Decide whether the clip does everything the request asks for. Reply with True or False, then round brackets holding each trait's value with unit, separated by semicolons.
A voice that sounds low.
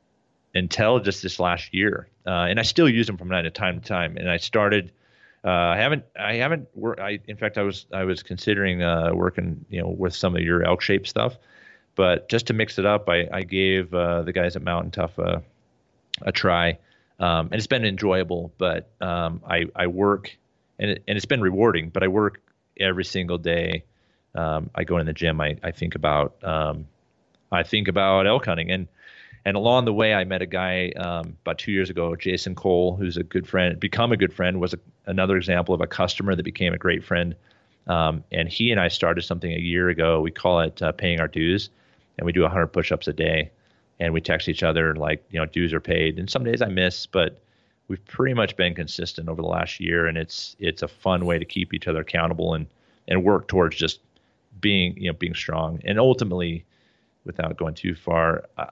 True (90 Hz)